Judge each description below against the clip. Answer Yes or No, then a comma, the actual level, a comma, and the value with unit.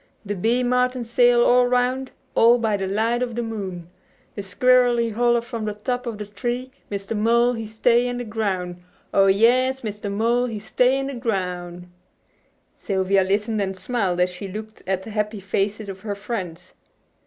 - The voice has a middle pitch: No, high, 220 Hz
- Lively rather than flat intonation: No, average, 3.6 semitones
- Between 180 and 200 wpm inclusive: Yes, average, 190 wpm